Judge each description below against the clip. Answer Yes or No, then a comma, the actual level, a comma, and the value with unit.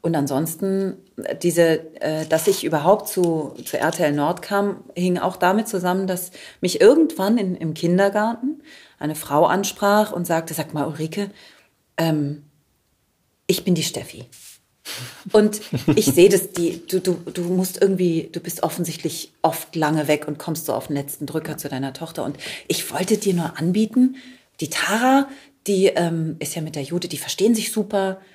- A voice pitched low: No, medium, 175 Hz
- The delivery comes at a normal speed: Yes, average, 165 wpm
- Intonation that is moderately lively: Yes, average, 4.0 semitones